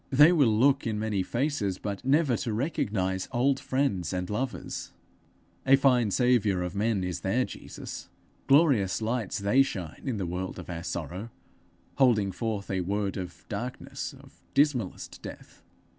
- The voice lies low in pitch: Yes, low, 110 Hz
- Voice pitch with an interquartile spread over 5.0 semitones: Yes, wide, 5.6 semitones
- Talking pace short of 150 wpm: No, average, 155 wpm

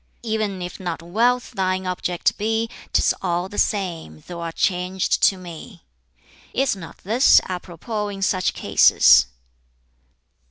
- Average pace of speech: No, slow, 125 wpm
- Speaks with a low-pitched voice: No, medium, 185 Hz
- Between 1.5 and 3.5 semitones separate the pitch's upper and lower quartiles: Yes, average, 3.1 semitones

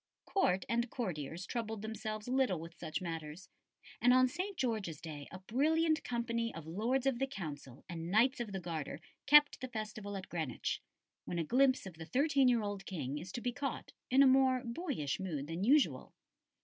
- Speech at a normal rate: Yes, average, 190 wpm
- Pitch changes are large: Yes, wide, 7.2 semitones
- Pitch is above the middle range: Yes, high, 215 Hz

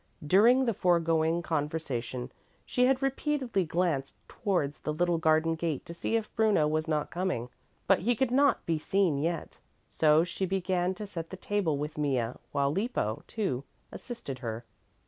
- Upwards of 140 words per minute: Yes, average, 165 wpm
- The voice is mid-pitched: Yes, medium, 170 Hz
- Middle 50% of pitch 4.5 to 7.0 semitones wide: Yes, average, 5.1 semitones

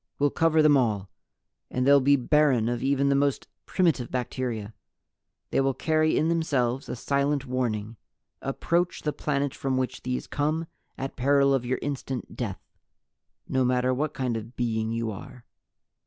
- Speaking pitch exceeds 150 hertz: No, low, 130 Hz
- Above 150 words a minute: Yes, average, 160 wpm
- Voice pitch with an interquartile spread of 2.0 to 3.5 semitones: Yes, average, 2.7 semitones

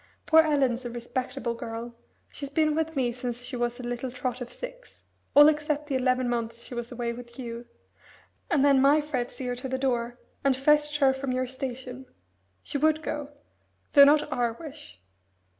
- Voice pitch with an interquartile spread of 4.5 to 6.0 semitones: No, average, 3.2 semitones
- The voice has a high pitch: Yes, very high, 260 Hz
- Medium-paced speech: Yes, average, 190 wpm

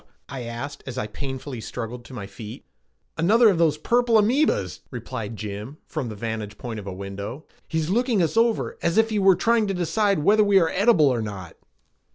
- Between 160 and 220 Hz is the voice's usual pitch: No, medium, 140 Hz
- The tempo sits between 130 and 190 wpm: No, average, 200 wpm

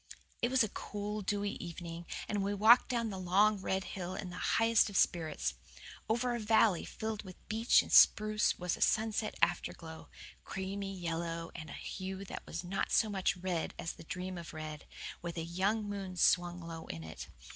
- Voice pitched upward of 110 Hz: Yes, high, 190 Hz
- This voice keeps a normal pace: Yes, average, 190 wpm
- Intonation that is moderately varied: Yes, average, 3.6 semitones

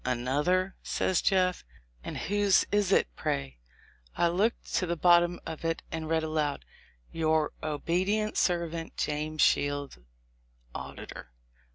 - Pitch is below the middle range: No, medium, 165 Hz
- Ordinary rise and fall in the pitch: Yes, average, 3.4 semitones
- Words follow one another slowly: Yes, slow, 130 wpm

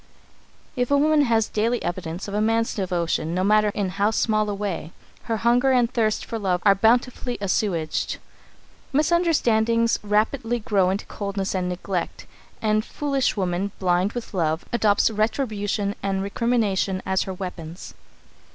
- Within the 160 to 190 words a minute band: No, average, 150 wpm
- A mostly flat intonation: No, average, 3.5 semitones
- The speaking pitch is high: Yes, high, 210 Hz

